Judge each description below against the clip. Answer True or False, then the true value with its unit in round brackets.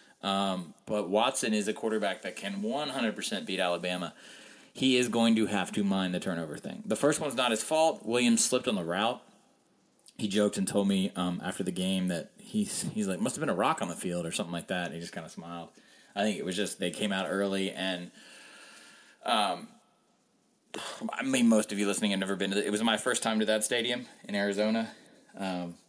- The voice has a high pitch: False (105 Hz)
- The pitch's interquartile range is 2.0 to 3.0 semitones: False (4.8 semitones)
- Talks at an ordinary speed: False (225 wpm)